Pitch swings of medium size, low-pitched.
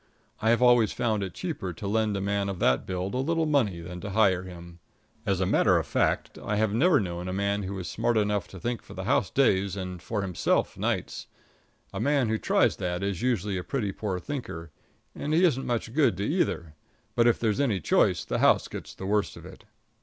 Yes: average, 4.4 semitones; low, 100 Hz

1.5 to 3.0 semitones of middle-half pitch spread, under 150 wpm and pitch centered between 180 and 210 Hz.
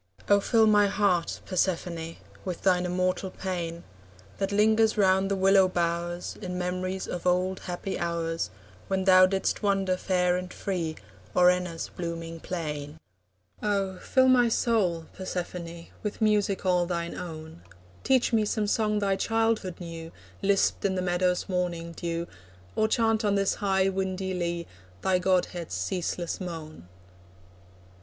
Yes: narrow, 2.4 semitones; average, 140 wpm; medium, 185 Hz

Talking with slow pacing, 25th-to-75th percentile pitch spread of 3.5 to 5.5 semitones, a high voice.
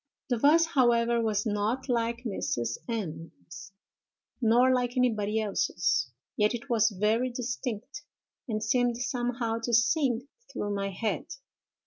No: slow, 125 wpm; average, 2.9 semitones; high, 230 Hz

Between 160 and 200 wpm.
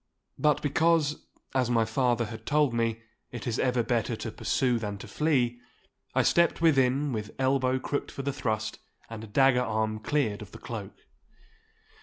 Yes: average, 165 wpm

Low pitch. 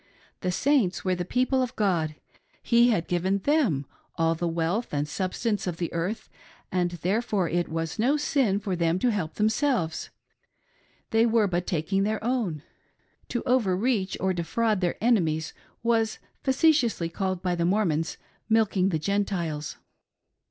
No: high, 190 Hz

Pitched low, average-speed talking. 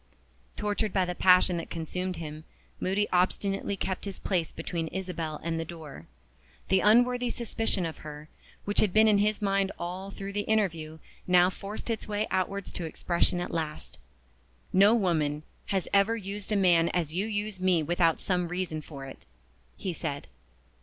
No: medium, 185 Hz; average, 165 wpm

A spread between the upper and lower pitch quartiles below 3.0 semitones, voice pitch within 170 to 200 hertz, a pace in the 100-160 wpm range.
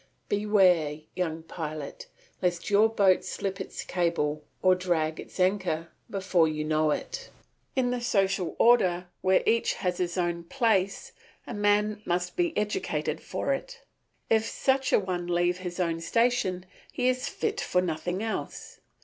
No: average, 3.5 semitones; medium, 185 Hz; average, 150 wpm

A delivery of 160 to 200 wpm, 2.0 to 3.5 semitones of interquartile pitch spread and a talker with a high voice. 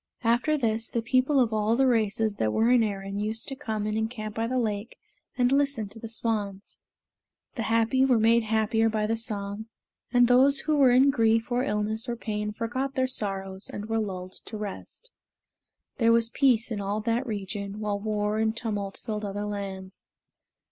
Yes: average, 190 wpm; narrow, 2.6 semitones; high, 220 Hz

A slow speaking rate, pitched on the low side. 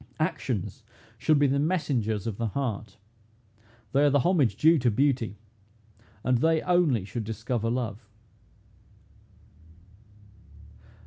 Yes: slow, 115 wpm; low, 125 Hz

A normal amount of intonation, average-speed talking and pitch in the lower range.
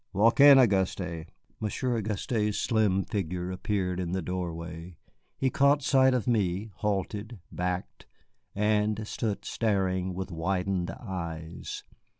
No: average, 3.3 semitones; slow, 120 wpm; very low, 95 Hz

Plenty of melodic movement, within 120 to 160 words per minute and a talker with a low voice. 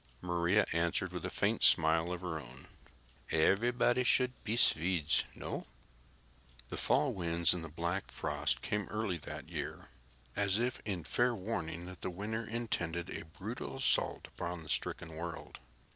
No: average, 4.8 semitones; average, 155 wpm; very low, 90 Hz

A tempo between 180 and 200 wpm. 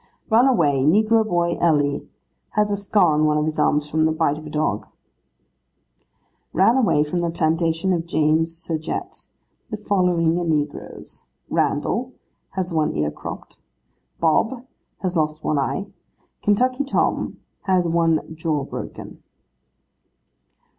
No: slow, 135 wpm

